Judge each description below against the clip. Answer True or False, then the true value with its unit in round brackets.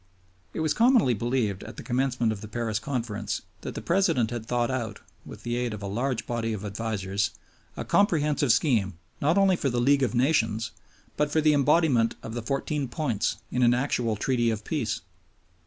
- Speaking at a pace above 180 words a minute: True (190 wpm)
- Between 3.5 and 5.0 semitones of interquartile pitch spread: True (4.2 semitones)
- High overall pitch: False (120 Hz)